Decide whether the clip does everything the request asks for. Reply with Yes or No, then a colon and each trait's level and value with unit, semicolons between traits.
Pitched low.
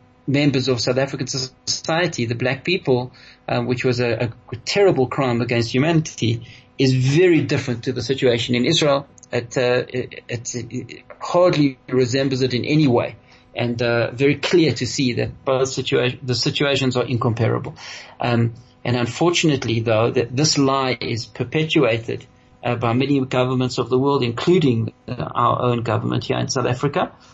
Yes: low, 125 Hz